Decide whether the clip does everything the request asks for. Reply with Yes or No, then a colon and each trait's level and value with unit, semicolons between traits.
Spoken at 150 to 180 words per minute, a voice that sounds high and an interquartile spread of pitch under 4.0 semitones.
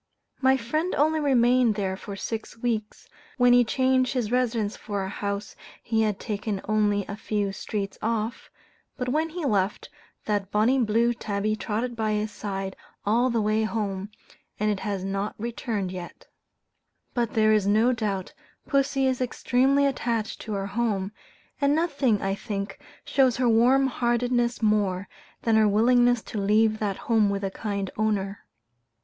Yes: average, 160 wpm; high, 220 Hz; average, 3.3 semitones